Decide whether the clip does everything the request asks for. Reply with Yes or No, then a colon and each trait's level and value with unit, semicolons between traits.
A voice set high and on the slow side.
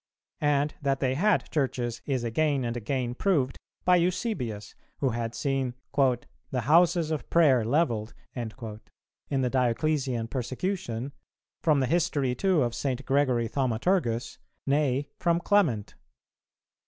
No: low, 135 Hz; slow, 125 wpm